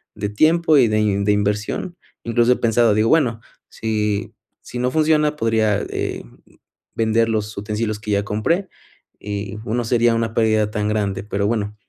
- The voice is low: Yes, low, 110 Hz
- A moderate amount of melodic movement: No, narrow, 2.3 semitones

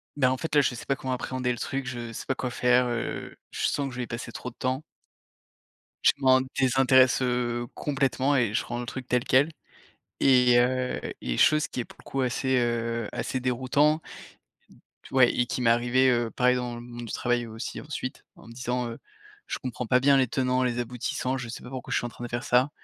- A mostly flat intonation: Yes, narrow, 1.4 semitones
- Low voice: Yes, low, 125 Hz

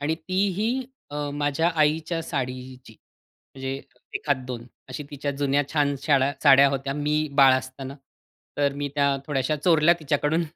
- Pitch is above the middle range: No, medium, 145 Hz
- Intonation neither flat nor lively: No, narrow, 2.3 semitones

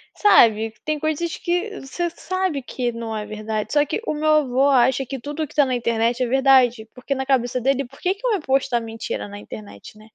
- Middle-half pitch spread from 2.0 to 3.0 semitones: No, average, 4.7 semitones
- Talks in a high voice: Yes, very high, 260 Hz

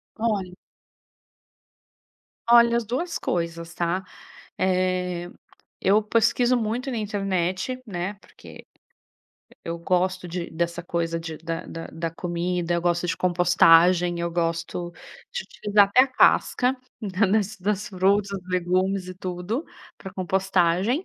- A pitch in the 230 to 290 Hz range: No, medium, 185 Hz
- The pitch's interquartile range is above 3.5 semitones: No, average, 3.2 semitones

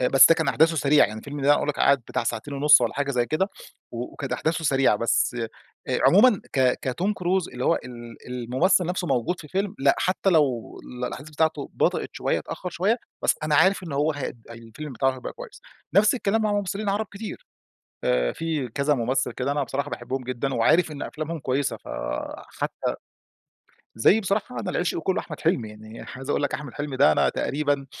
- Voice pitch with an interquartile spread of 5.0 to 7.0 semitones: Yes, average, 5.3 semitones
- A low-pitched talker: No, medium, 145 Hz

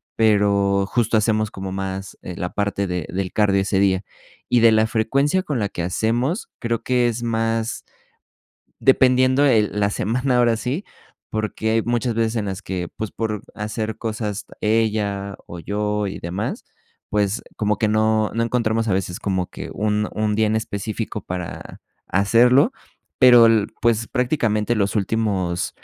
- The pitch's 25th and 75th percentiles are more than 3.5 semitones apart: No, narrow, 2.5 semitones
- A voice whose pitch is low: Yes, low, 110 Hz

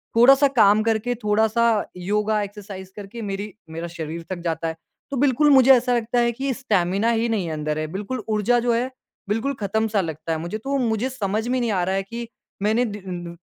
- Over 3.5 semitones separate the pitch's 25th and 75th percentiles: Yes, average, 3.9 semitones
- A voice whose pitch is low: No, high, 215 Hz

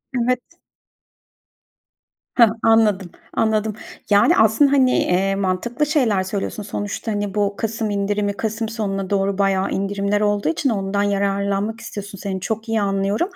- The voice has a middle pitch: No, high, 205 Hz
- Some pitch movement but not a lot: No, narrow, 2.1 semitones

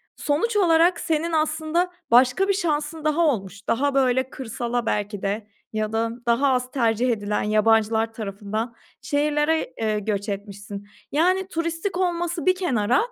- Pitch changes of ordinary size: No, wide, 7.0 semitones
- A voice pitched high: Yes, very high, 255 Hz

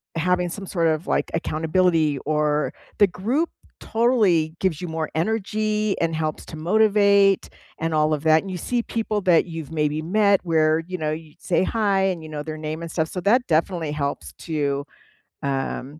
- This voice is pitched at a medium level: Yes, medium, 165 Hz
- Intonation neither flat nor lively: Yes, average, 4.3 semitones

